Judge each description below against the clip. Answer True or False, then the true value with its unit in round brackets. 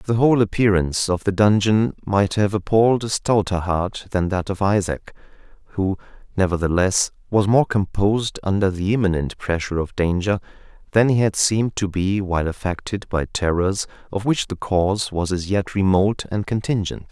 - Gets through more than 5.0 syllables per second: True (5.2 syllables/s)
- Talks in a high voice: False (100 Hz)